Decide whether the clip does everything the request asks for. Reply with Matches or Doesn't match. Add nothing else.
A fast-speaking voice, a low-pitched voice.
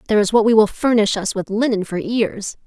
Doesn't match